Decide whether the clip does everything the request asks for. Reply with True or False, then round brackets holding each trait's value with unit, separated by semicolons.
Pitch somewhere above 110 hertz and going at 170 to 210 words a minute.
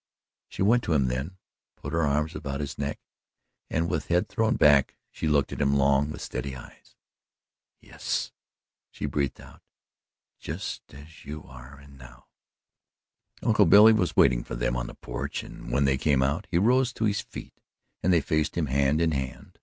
False (75 Hz; 185 wpm)